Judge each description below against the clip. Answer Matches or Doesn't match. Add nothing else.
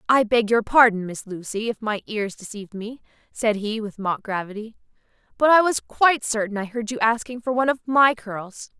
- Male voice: Doesn't match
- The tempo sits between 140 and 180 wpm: Doesn't match